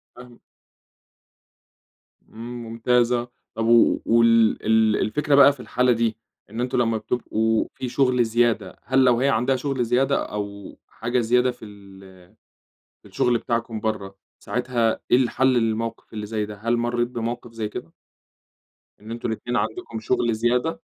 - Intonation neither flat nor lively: No, narrow, 1.8 semitones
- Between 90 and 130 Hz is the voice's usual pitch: Yes, low, 115 Hz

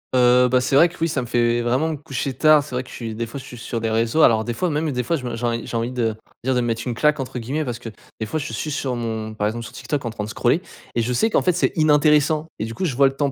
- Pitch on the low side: Yes, low, 125 Hz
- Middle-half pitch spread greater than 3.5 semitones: Yes, average, 4.2 semitones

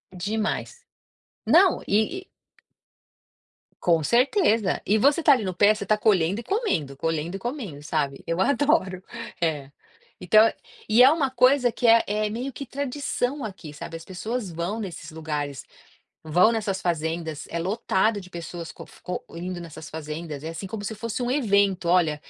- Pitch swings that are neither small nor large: No, wide, 6.0 semitones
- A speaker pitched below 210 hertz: Yes, high, 195 Hz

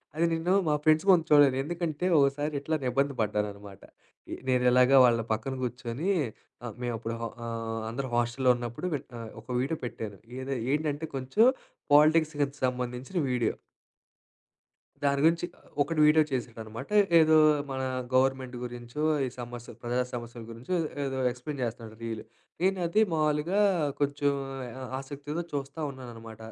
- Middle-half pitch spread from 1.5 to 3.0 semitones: No, average, 4.1 semitones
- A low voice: Yes, low, 130 Hz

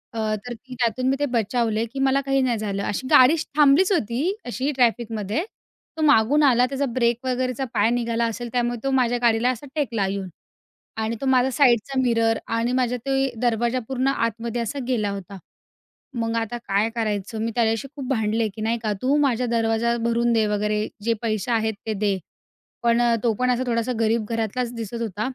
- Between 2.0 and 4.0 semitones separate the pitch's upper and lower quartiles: Yes, narrow, 2.4 semitones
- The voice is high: Yes, high, 235 Hz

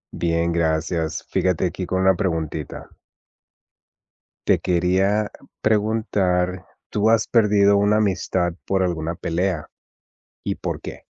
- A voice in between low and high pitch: No, very low, 95 Hz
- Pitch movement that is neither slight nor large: Yes, average, 3.2 semitones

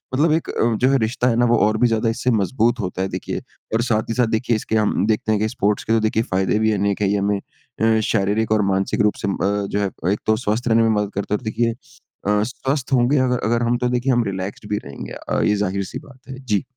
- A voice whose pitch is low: Yes, low, 110 Hz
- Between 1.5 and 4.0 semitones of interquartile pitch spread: Yes, average, 2.9 semitones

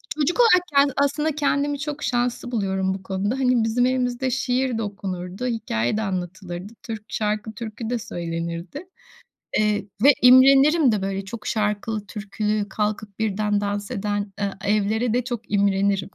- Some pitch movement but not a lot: Yes, average, 3.9 semitones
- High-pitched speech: Yes, high, 215 Hz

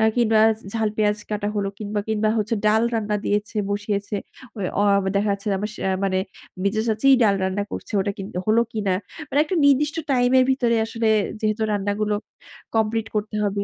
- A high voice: Yes, high, 215 Hz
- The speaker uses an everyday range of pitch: No, narrow, 1.7 semitones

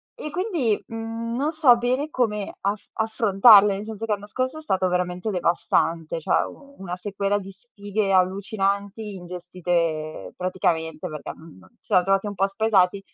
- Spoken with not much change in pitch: No, average, 3.5 semitones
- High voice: Yes, high, 200 Hz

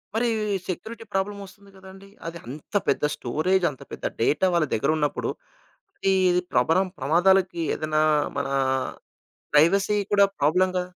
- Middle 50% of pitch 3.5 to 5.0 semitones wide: Yes, average, 4.0 semitones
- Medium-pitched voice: Yes, medium, 180 Hz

